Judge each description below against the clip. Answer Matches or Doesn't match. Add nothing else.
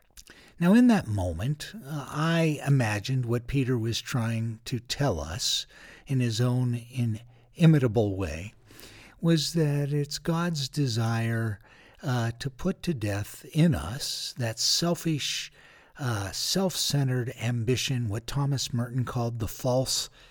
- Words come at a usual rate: Doesn't match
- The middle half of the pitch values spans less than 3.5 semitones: Doesn't match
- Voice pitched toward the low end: Matches